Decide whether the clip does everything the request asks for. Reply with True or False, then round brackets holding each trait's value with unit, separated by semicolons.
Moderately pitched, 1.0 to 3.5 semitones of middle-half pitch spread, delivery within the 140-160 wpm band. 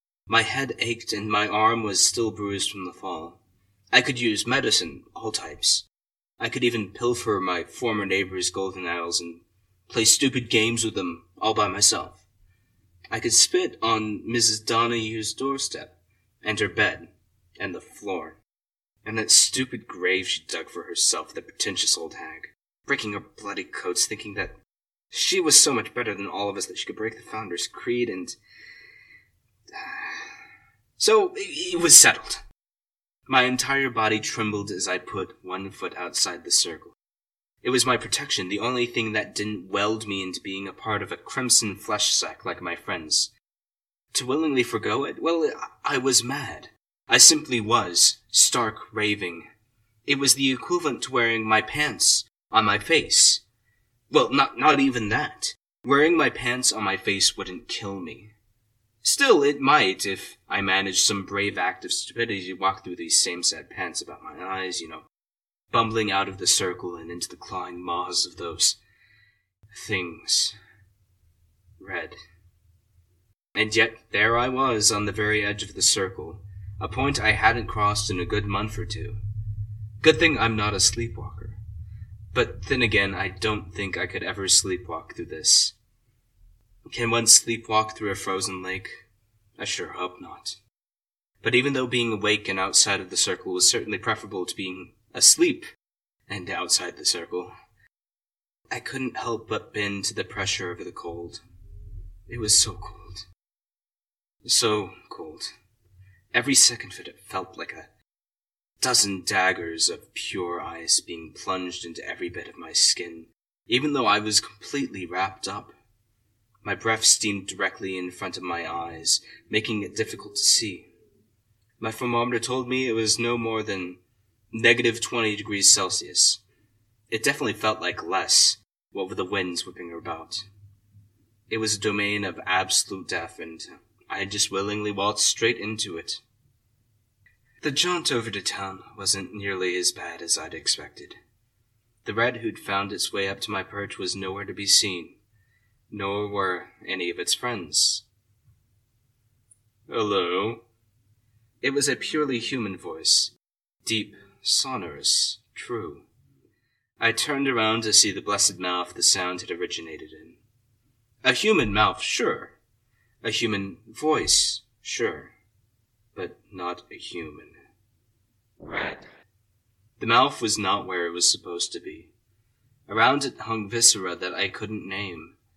False (105 Hz; 3.1 semitones; 155 wpm)